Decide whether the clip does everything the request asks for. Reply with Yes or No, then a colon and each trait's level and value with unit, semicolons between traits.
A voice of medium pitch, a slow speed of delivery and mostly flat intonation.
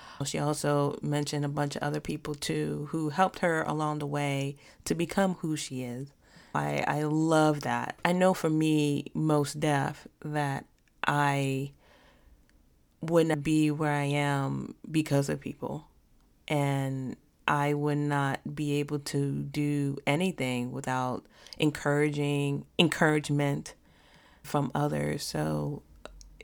Yes: medium, 145 Hz; slow, 125 wpm; narrow, 1.8 semitones